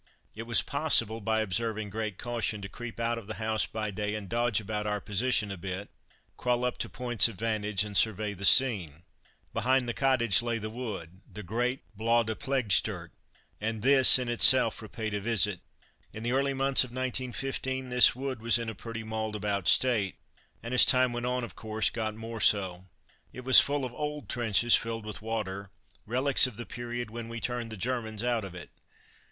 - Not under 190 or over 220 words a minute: Yes, average, 195 wpm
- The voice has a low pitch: Yes, low, 115 Hz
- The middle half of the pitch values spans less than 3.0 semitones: Yes, narrow, 2.6 semitones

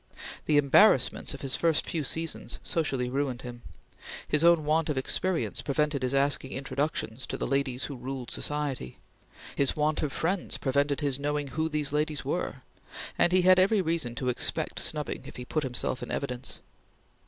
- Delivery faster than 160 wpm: Yes, average, 175 wpm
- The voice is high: No, medium, 145 Hz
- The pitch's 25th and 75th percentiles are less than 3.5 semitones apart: Yes, average, 3.0 semitones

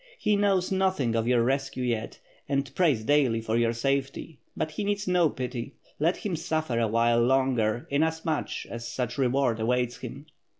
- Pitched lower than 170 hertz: Yes, low, 135 Hz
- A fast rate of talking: No, average, 185 wpm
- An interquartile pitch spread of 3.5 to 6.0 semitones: Yes, average, 5.2 semitones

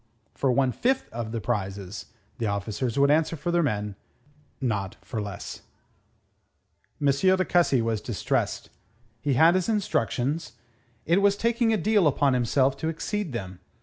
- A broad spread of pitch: Yes, wide, 7.5 semitones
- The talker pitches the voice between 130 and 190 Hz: Yes, low, 135 Hz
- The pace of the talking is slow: No, average, 150 wpm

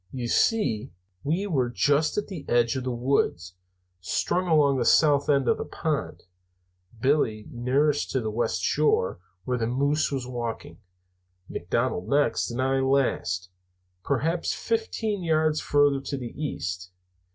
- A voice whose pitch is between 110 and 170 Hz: Yes, low, 135 Hz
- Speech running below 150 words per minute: Yes, average, 140 wpm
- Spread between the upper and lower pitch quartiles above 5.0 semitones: No, average, 4.1 semitones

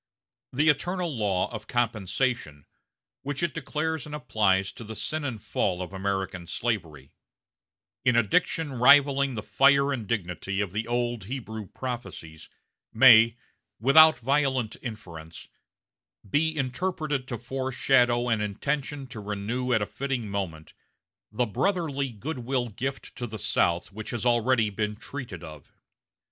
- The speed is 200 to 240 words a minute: No, slow, 135 wpm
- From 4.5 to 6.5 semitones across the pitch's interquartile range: Yes, average, 4.8 semitones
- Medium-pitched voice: No, low, 120 Hz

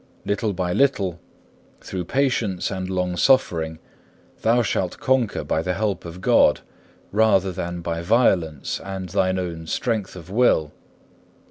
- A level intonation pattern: No, average, 3.8 semitones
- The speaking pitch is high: No, very low, 95 Hz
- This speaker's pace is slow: Yes, slow, 130 wpm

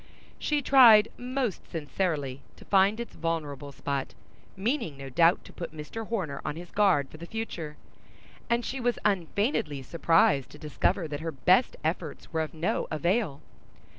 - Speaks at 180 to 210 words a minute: No, average, 160 wpm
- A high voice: No, medium, 170 Hz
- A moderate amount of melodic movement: No, wide, 6.2 semitones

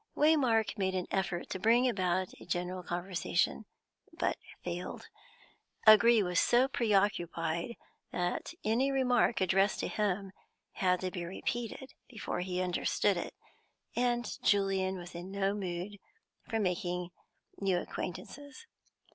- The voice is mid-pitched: No, high, 195 Hz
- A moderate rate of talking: No, slow, 125 wpm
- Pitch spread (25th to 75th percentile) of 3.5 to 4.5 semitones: Yes, average, 4.0 semitones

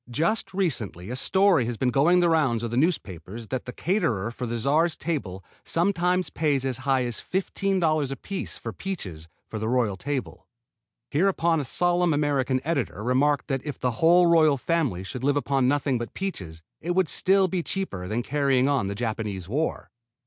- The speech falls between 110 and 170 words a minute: No, average, 180 wpm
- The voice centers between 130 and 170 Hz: Yes, medium, 140 Hz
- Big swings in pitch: Yes, wide, 6.1 semitones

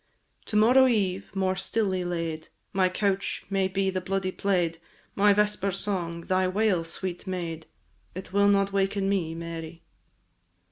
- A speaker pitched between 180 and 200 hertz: Yes, high, 190 Hz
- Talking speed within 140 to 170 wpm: Yes, average, 145 wpm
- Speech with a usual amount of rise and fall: No, narrow, 2.1 semitones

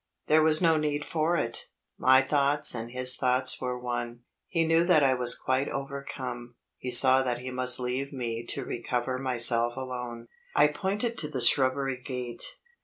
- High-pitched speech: No, low, 130 Hz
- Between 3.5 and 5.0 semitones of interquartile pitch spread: No, average, 2.9 semitones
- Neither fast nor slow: Yes, average, 175 wpm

